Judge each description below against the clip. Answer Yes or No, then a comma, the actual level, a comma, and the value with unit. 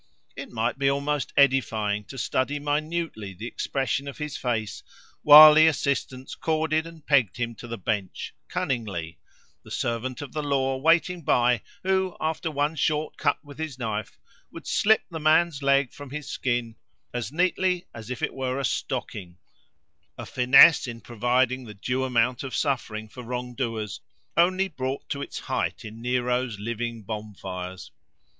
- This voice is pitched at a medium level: No, low, 130 Hz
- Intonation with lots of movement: No, average, 4.4 semitones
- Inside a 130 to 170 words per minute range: Yes, average, 160 wpm